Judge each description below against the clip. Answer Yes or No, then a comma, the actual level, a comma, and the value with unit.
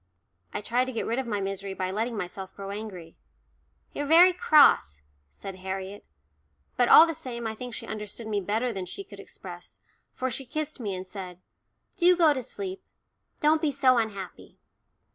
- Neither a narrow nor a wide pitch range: No, wide, 6.4 semitones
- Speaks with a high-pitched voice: Yes, high, 225 Hz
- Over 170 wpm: Yes, average, 180 wpm